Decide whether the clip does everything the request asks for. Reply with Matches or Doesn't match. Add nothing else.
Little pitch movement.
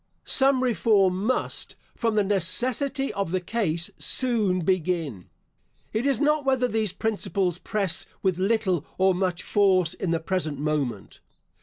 Doesn't match